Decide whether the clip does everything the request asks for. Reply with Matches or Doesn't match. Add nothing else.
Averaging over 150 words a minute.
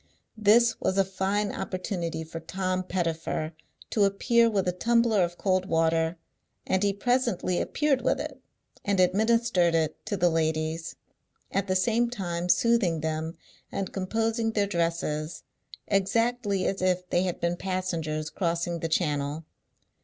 Doesn't match